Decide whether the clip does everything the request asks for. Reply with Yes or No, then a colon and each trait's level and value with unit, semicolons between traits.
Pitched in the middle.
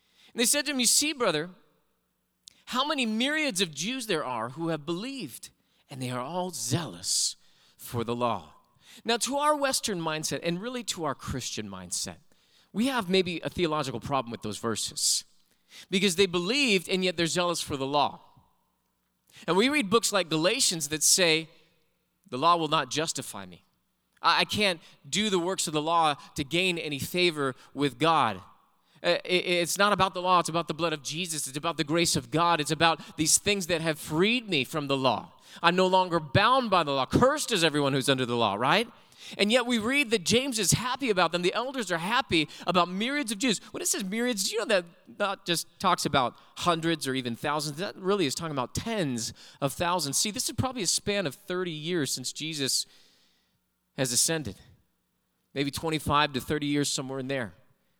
Yes: medium, 170 Hz